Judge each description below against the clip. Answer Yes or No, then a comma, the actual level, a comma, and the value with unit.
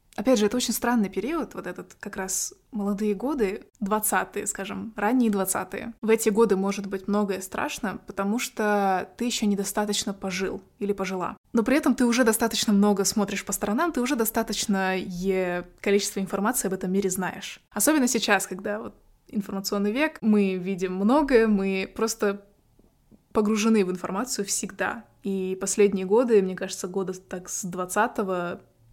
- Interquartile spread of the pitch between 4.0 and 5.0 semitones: No, narrow, 2.5 semitones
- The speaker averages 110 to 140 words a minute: No, average, 155 wpm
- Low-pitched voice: No, high, 205 Hz